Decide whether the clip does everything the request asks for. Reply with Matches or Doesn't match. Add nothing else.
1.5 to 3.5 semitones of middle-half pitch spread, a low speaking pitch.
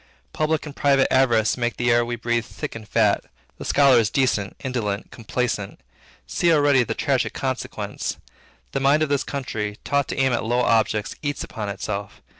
Doesn't match